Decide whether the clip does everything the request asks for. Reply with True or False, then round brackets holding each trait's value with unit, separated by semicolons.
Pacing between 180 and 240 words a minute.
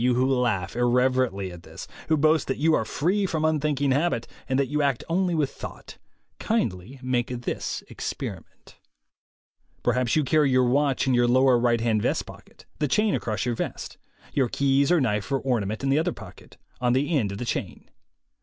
True (195 wpm)